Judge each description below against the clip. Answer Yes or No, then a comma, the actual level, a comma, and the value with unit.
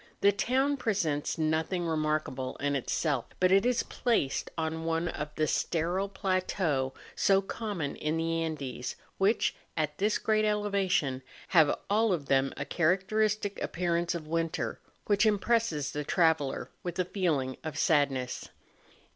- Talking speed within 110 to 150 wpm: Yes, average, 140 wpm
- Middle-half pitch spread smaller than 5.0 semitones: Yes, average, 4.6 semitones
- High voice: No, medium, 165 Hz